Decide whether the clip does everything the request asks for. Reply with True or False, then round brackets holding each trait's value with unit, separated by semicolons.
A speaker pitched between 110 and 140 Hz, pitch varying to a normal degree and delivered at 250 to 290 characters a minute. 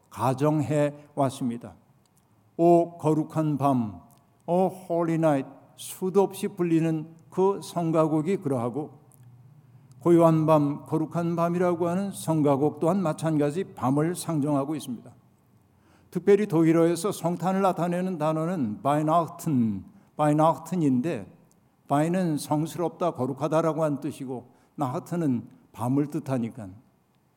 False (155 Hz; 3.4 semitones; 270 characters per minute)